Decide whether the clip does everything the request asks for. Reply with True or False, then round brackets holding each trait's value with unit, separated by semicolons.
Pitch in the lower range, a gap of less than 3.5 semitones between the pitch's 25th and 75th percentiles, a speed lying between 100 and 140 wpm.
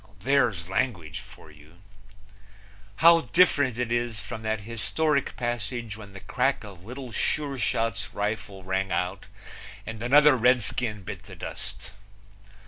False (115 Hz; 4.6 semitones; 135 wpm)